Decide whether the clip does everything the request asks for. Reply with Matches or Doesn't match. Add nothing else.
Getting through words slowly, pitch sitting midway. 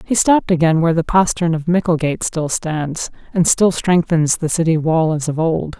Doesn't match